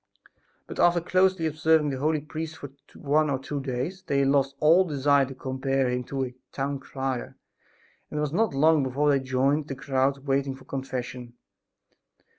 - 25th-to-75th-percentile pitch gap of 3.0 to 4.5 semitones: No, narrow, 2.5 semitones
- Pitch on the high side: No, medium, 140 Hz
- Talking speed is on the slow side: No, average, 175 wpm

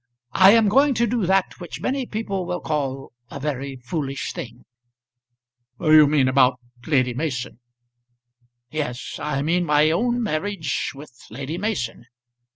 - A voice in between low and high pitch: Yes, medium, 155 Hz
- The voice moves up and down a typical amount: No, wide, 6.2 semitones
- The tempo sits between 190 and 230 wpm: No, average, 140 wpm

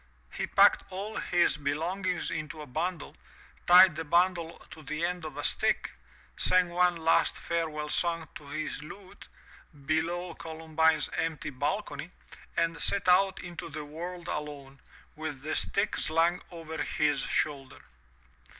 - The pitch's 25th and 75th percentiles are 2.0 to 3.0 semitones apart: Yes, narrow, 2.6 semitones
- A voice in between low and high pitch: Yes, medium, 165 Hz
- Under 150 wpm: Yes, average, 140 wpm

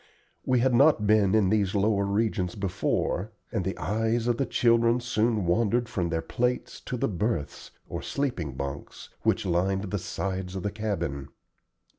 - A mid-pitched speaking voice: No, low, 105 Hz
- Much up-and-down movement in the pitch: No, average, 4.0 semitones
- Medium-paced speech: Yes, average, 165 wpm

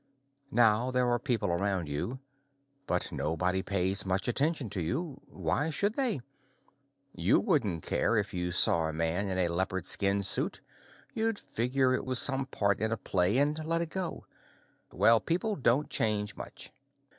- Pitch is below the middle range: Yes, low, 110 Hz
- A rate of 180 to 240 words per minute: No, average, 165 wpm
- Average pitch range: No, wide, 6.9 semitones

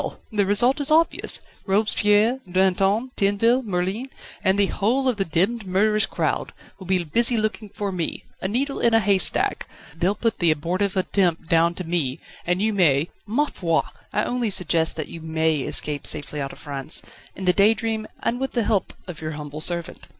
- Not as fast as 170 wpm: No, average, 185 wpm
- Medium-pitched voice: No, high, 195 Hz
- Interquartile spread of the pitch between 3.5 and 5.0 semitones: Yes, average, 4.7 semitones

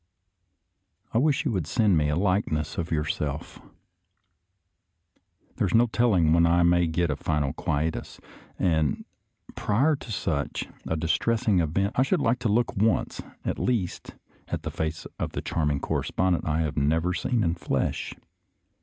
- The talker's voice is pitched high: No, very low, 85 Hz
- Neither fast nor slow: Yes, average, 165 wpm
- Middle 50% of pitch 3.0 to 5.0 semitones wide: No, wide, 5.4 semitones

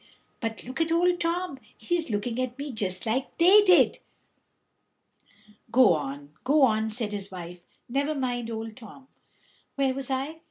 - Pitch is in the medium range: No, very high, 255 Hz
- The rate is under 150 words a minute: No, average, 155 wpm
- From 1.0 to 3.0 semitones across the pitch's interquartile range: No, average, 5.2 semitones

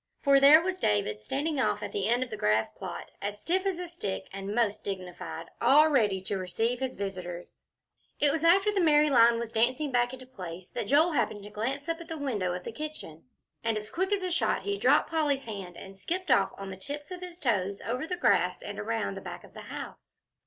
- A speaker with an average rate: No, fast, 230 wpm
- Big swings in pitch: Yes, wide, 8.1 semitones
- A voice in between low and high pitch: No, high, 245 Hz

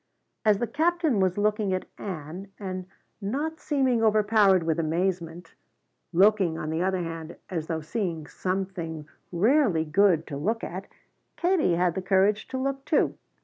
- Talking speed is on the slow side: No, average, 150 wpm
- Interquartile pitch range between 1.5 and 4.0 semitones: No, average, 4.5 semitones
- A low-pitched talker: No, high, 190 Hz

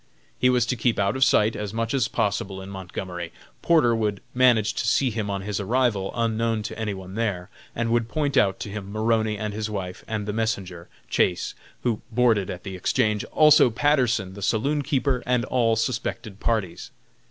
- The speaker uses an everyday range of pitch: Yes, average, 3.2 semitones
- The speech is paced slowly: No, average, 190 wpm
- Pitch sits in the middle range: No, low, 110 Hz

